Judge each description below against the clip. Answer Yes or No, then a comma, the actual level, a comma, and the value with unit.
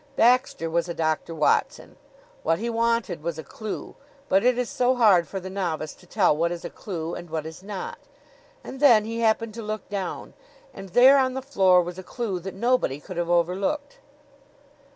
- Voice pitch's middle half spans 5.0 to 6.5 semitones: Yes, wide, 5.4 semitones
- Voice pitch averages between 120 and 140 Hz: No, high, 195 Hz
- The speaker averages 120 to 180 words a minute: No, average, 195 wpm